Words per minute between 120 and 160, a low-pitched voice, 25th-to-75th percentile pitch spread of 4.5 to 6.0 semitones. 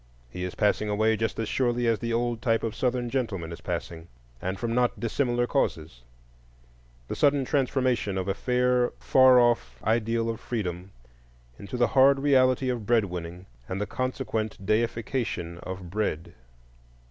Yes: average, 155 wpm; low, 115 Hz; average, 5.3 semitones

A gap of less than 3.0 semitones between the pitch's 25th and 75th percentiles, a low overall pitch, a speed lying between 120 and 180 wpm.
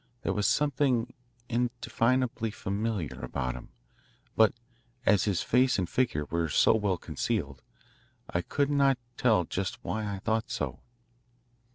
No: wide, 5.6 semitones; low, 110 Hz; slow, 135 wpm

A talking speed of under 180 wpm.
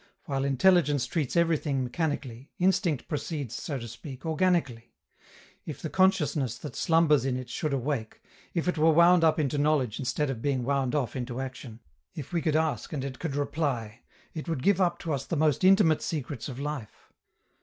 No: average, 185 wpm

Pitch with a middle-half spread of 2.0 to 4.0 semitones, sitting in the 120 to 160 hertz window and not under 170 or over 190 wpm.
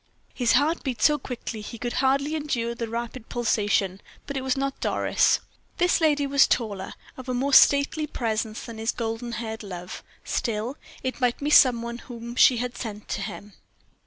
No: average, 3.5 semitones; high, 240 Hz; average, 185 wpm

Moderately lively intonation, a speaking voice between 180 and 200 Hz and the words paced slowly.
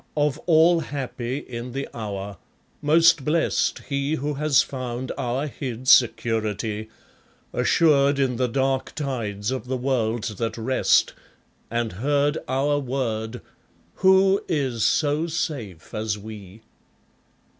No: average, 4.3 semitones; low, 130 Hz; slow, 120 wpm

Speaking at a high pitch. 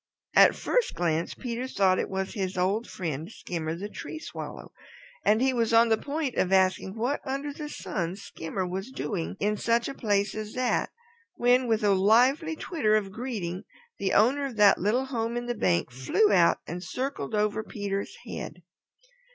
Yes: high, 215 Hz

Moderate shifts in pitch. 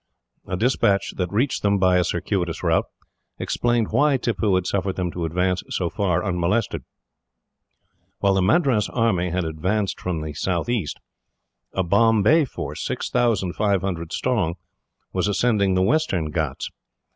Yes: average, 4.2 semitones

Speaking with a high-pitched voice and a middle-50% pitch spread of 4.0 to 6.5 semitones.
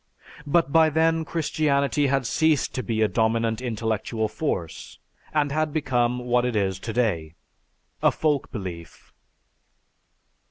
No: low, 125 Hz; average, 5.3 semitones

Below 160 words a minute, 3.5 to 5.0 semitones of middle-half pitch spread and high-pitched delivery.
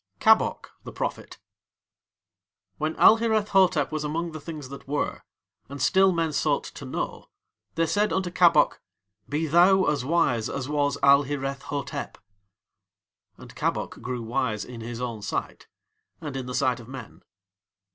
No: average, 145 wpm; average, 4.5 semitones; medium, 145 Hz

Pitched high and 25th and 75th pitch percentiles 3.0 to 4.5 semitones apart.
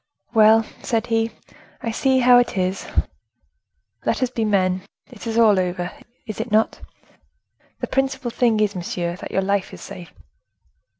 Yes: high, 220 Hz; average, 4.1 semitones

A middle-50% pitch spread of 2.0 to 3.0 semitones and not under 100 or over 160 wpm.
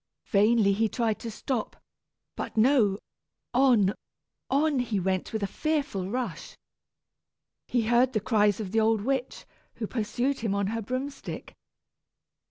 No: average, 3.8 semitones; average, 145 wpm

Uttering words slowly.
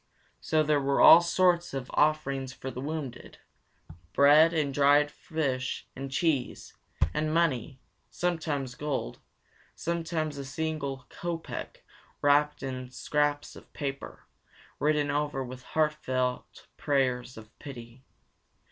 Yes: slow, 115 wpm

